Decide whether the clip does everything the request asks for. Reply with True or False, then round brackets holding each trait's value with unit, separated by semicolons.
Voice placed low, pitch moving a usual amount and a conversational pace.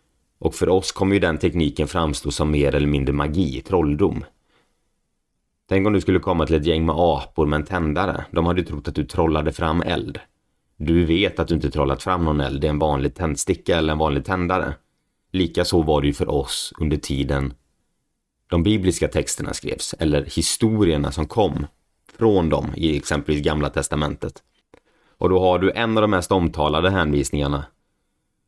True (80 Hz; 3.6 semitones; 180 wpm)